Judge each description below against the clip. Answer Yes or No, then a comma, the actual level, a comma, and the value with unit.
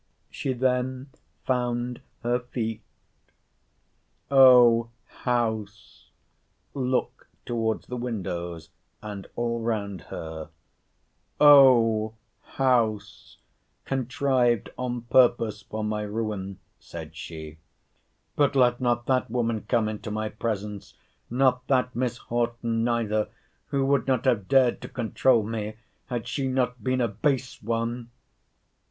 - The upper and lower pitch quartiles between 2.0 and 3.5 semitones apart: Yes, average, 2.8 semitones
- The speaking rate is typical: No, slow, 105 wpm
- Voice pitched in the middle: No, low, 120 Hz